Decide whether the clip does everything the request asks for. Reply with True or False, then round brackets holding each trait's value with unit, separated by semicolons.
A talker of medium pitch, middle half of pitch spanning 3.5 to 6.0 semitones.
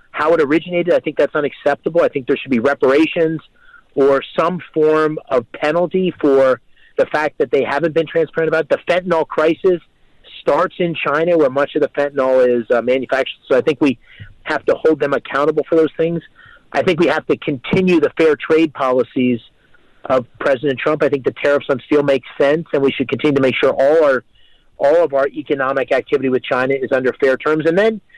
True (155 Hz; 4.1 semitones)